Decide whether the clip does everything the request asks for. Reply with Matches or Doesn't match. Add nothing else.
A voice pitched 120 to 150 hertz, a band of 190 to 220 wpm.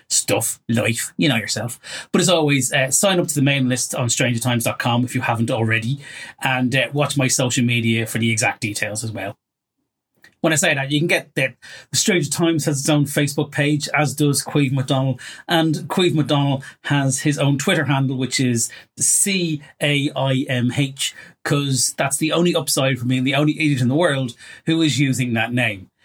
Matches